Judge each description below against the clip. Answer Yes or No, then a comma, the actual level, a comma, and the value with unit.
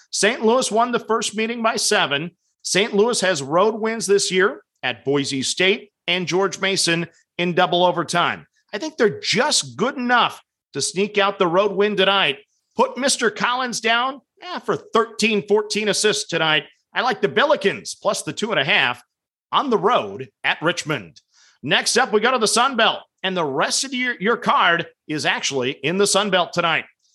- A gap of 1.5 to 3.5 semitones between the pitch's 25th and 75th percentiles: No, average, 4.3 semitones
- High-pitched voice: Yes, high, 200 Hz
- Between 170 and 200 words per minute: Yes, average, 185 wpm